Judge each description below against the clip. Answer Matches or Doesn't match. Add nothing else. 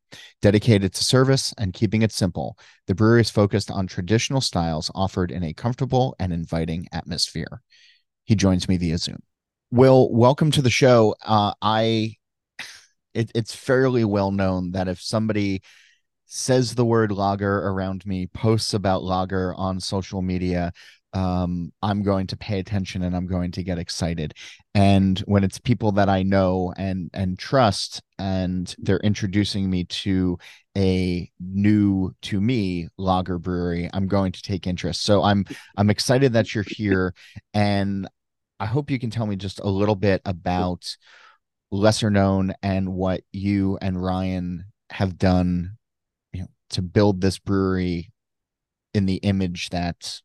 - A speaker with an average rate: Matches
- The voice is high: Doesn't match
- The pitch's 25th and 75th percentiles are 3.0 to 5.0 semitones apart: Doesn't match